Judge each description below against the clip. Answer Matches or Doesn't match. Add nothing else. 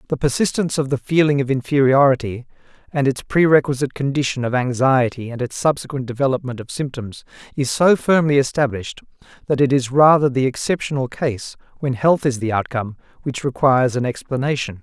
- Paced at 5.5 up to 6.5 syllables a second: Matches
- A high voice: Doesn't match